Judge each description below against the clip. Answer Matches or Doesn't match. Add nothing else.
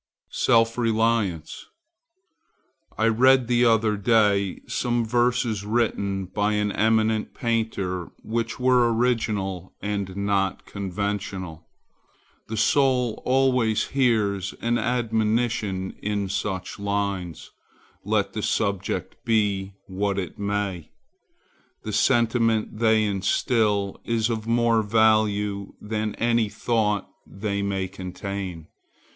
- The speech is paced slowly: Matches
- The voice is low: Matches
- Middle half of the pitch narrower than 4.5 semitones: Matches